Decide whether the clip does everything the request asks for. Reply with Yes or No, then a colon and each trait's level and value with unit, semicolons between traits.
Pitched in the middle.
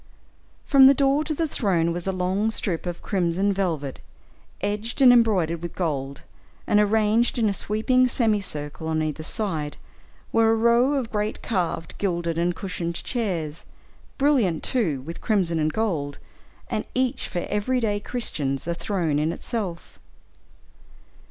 No: high, 195 Hz